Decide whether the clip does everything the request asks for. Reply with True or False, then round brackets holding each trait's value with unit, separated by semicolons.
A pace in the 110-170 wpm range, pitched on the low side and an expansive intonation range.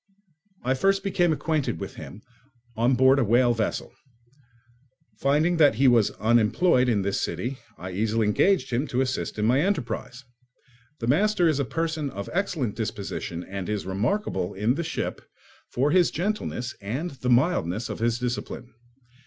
True (160 wpm; 125 Hz; 6.1 semitones)